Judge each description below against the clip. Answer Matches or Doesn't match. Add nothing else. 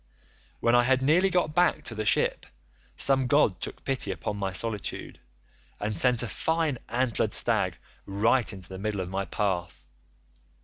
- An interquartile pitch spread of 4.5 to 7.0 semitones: Matches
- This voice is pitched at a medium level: Doesn't match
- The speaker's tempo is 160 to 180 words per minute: Matches